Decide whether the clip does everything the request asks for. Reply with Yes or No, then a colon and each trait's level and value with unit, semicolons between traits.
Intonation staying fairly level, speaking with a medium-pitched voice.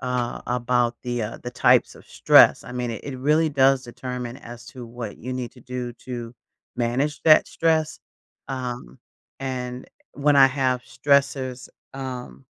No: narrow, 1.8 semitones; low, 125 Hz